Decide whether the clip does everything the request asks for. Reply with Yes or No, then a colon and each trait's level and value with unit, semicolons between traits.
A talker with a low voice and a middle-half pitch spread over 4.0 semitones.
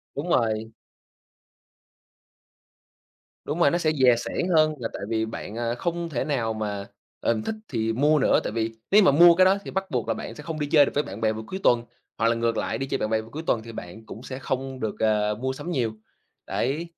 Yes: low, 125 Hz; wide, 5.6 semitones